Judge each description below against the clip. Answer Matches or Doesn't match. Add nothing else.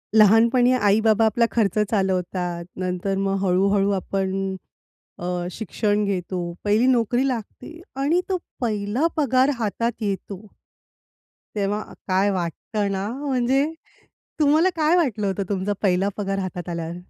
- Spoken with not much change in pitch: Doesn't match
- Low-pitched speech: Doesn't match